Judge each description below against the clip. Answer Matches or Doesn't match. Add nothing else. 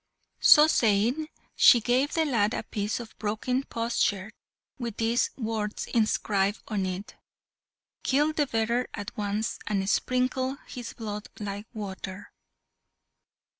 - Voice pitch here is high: Matches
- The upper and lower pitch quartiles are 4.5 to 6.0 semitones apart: Doesn't match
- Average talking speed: Doesn't match